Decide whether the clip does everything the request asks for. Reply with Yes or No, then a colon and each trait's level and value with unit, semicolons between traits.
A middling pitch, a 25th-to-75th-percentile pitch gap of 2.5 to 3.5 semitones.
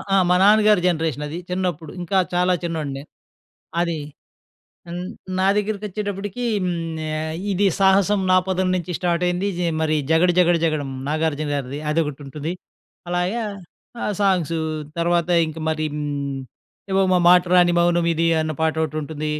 Yes: medium, 170 Hz; average, 2.9 semitones